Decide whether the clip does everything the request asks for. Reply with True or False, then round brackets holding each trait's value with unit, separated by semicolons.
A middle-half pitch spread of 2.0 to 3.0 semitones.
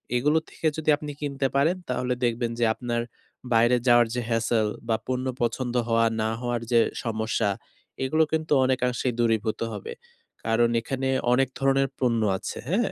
True (2.7 semitones)